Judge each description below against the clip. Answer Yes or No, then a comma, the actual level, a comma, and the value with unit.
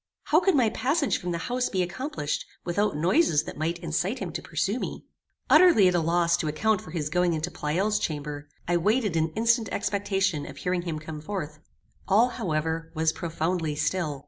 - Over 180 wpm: Yes, average, 190 wpm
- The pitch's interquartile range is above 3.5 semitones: Yes, average, 4.7 semitones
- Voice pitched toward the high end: No, medium, 175 Hz